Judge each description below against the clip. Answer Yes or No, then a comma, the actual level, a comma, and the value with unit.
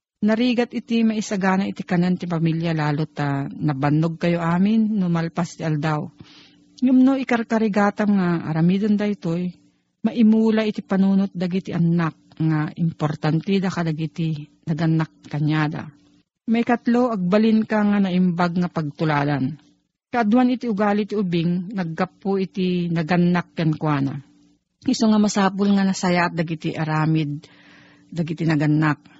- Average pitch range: Yes, average, 4.7 semitones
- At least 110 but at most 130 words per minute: Yes, average, 125 wpm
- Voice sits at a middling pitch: Yes, medium, 175 Hz